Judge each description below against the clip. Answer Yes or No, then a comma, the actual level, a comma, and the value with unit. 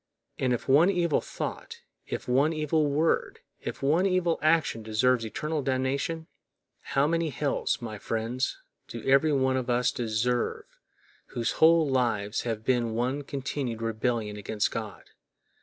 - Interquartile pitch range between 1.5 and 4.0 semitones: No, average, 4.6 semitones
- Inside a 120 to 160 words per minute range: Yes, average, 140 wpm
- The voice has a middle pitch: No, low, 130 Hz